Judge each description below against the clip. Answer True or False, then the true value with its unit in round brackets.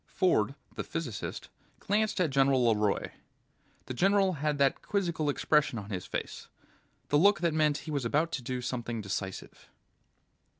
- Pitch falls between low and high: True (145 Hz)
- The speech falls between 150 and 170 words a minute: True (155 wpm)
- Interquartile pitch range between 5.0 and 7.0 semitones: True (5.6 semitones)